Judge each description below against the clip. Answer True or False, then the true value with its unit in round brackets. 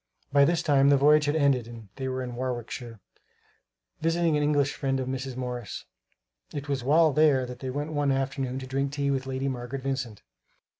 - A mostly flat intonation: True (2.1 semitones)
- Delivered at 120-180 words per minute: False (195 wpm)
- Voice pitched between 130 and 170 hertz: True (135 Hz)